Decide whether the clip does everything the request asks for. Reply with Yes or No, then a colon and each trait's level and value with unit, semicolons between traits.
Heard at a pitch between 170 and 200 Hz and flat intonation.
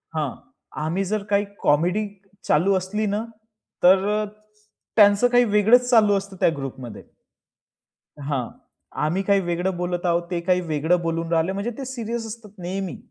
No: high, 190 Hz; average, 3.7 semitones